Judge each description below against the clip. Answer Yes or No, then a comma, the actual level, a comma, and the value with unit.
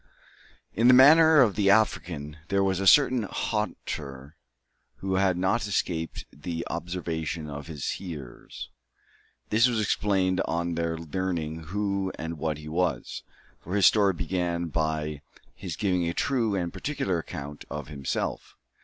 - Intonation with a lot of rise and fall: No, average, 3.9 semitones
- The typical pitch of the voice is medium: No, very low, 90 Hz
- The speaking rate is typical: Yes, average, 145 wpm